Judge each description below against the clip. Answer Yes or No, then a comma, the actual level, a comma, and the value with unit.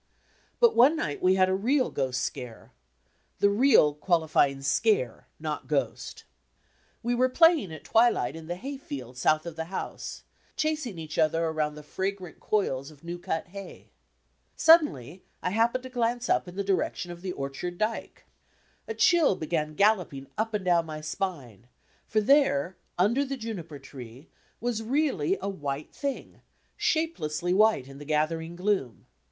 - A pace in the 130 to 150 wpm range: No, average, 165 wpm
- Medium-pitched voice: Yes, medium, 180 Hz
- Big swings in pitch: Yes, wide, 7.3 semitones